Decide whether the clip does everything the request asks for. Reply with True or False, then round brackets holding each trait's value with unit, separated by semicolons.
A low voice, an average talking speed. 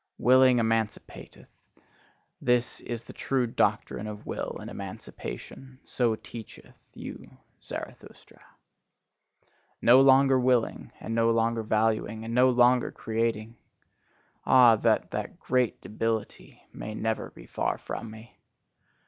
False (115 Hz; 115 wpm)